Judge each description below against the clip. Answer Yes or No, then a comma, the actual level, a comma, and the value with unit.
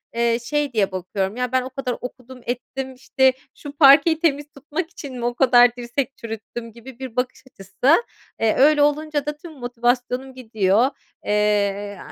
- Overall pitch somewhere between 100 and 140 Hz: No, very high, 250 Hz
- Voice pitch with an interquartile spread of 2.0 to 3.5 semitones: Yes, average, 3.2 semitones